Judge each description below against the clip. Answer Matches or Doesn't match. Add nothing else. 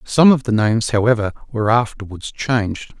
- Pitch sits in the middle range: Doesn't match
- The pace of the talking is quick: Doesn't match